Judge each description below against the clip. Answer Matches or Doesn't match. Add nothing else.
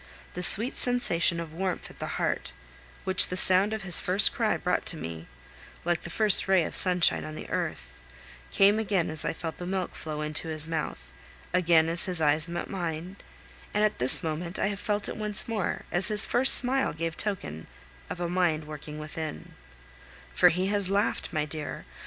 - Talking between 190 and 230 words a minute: Matches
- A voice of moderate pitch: Matches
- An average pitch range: Matches